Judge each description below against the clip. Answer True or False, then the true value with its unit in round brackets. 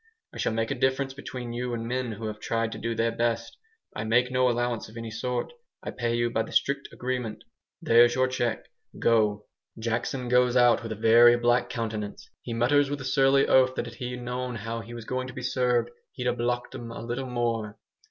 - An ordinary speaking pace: False (220 wpm)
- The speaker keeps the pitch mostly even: True (1.7 semitones)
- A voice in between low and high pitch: False (120 Hz)